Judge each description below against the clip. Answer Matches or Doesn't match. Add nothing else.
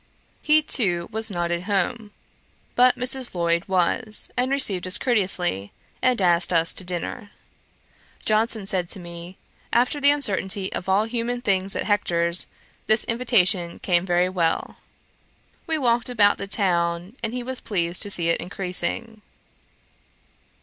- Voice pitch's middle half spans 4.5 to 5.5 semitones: Matches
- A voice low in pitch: Doesn't match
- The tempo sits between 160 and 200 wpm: Doesn't match